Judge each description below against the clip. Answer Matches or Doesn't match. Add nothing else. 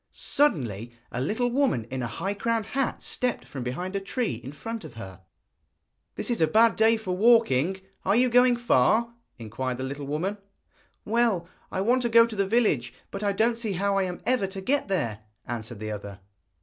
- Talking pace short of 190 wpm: Doesn't match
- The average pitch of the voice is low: Doesn't match